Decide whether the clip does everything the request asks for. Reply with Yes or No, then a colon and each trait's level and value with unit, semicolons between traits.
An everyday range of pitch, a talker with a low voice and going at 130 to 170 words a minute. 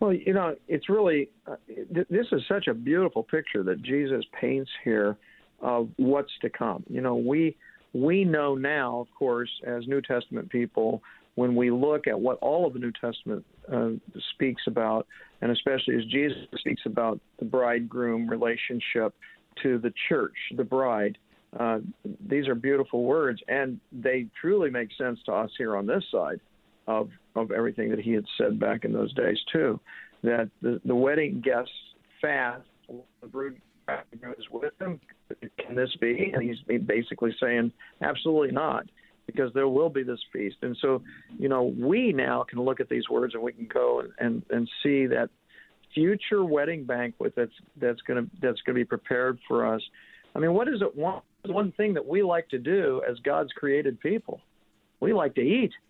No: average, 3.5 semitones; low, 130 Hz; average, 180 wpm